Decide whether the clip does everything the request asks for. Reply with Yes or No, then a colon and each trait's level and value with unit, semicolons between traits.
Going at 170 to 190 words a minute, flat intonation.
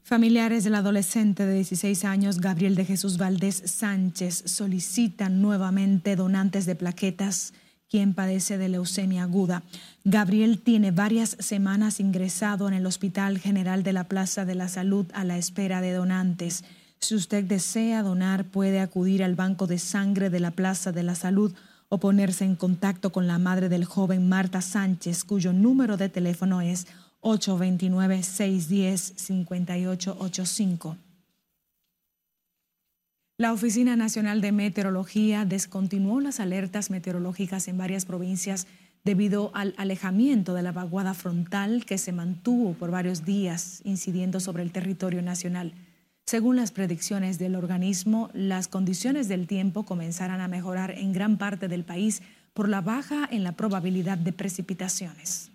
No: average, 140 wpm; narrow, 1.6 semitones